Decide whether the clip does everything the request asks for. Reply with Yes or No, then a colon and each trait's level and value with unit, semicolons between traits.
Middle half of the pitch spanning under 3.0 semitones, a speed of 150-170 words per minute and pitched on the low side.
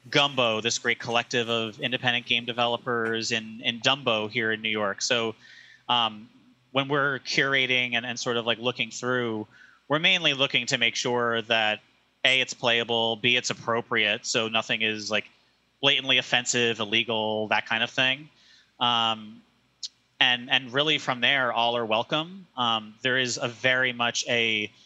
Yes: narrow, 2.4 semitones; average, 160 wpm; low, 120 Hz